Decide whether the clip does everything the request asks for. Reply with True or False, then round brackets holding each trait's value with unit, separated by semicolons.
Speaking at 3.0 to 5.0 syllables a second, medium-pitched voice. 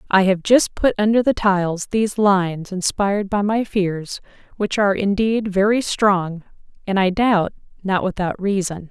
False (4.6 syllables/s; 195 Hz)